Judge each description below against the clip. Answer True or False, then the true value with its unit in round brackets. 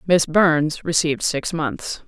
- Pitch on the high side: False (160 Hz)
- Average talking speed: True (145 wpm)